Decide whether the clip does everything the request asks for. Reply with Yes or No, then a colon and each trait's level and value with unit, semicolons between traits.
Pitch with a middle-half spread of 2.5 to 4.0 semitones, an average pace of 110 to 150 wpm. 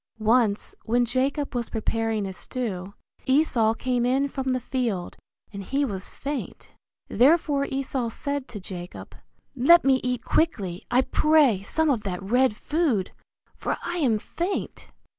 No: average, 4.5 semitones; average, 145 wpm